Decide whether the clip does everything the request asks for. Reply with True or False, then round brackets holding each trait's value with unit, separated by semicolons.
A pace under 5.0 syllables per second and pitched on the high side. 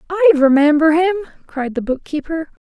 False (5.4 syllables/s; 315 Hz)